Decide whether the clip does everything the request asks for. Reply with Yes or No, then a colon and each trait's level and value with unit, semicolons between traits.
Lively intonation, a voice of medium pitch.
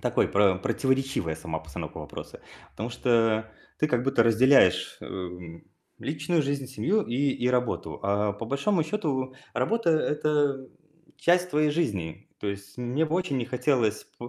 No: wide, 6.0 semitones; low, 130 Hz